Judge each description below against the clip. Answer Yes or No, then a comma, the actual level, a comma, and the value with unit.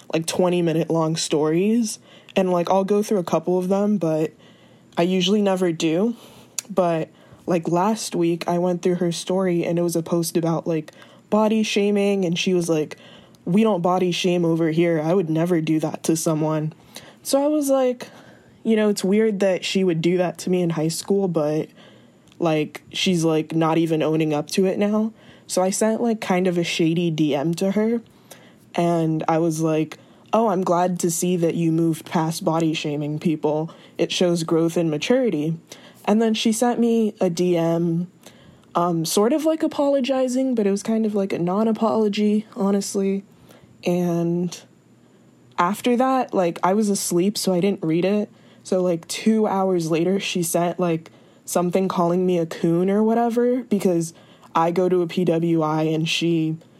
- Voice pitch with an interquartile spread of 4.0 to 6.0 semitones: No, average, 3.6 semitones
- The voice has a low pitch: No, medium, 180 Hz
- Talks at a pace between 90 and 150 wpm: No, average, 180 wpm